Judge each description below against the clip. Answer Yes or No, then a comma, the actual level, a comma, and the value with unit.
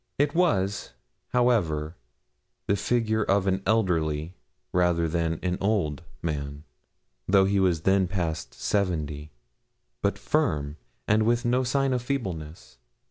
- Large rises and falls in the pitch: Yes, wide, 5.7 semitones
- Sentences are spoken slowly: Yes, slow, 125 wpm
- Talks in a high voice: No, very low, 95 Hz